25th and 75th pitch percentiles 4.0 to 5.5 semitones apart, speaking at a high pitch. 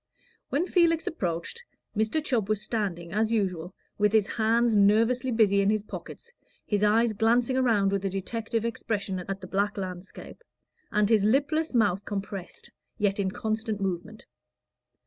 No: average, 2.8 semitones; high, 210 Hz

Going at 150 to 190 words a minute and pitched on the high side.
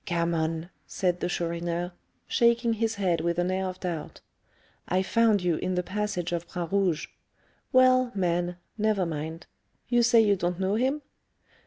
No: average, 160 wpm; medium, 180 Hz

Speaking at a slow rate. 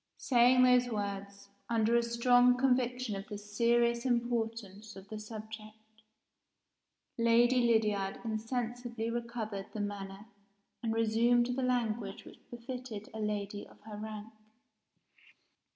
Yes: slow, 120 wpm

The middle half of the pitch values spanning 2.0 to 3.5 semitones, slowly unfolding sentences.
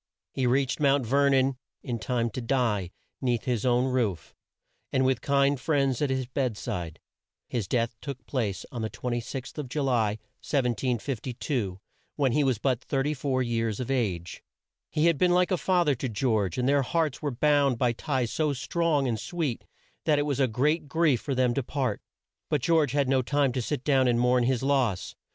No: average, 3.0 semitones; average, 195 wpm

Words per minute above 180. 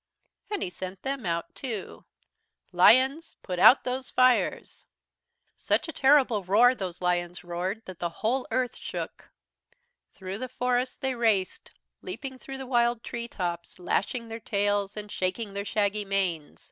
No: average, 150 wpm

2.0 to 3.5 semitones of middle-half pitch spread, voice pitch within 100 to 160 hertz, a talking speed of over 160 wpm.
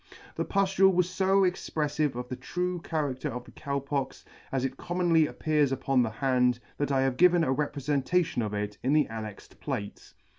No: average, 4.9 semitones; medium, 140 Hz; average, 185 wpm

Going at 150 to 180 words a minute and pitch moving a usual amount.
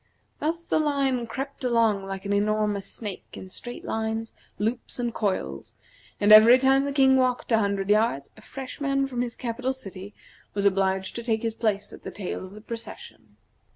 No: average, 190 wpm; average, 4.2 semitones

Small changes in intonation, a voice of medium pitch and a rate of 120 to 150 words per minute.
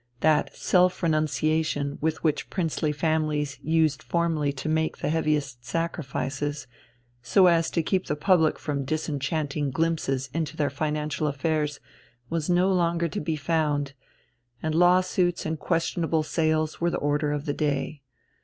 Yes: narrow, 2.1 semitones; medium, 155 Hz; average, 145 wpm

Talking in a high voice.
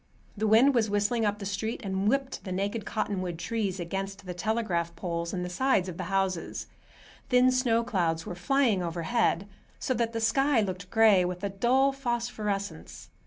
Yes: high, 205 Hz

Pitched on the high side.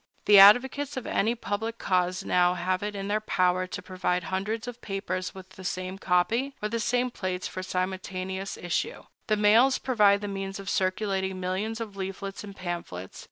Yes: high, 195 Hz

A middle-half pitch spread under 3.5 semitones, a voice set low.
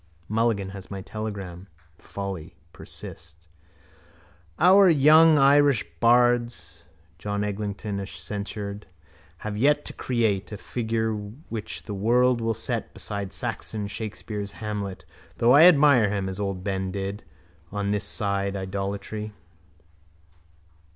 Yes: average, 3.0 semitones; low, 105 Hz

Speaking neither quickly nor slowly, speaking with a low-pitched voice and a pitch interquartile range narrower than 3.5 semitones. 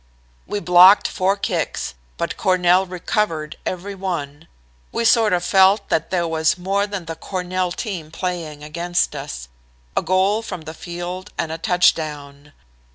No: average, 150 wpm; medium, 180 Hz; average, 2.9 semitones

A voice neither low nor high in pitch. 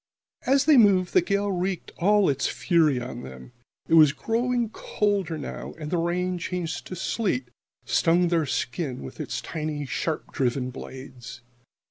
Yes: medium, 165 Hz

